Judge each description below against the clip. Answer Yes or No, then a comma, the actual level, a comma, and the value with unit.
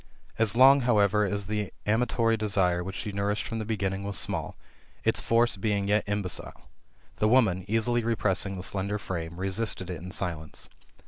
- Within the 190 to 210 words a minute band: No, average, 170 wpm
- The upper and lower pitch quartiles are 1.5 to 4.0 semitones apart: Yes, average, 2.8 semitones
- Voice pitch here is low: Yes, low, 100 Hz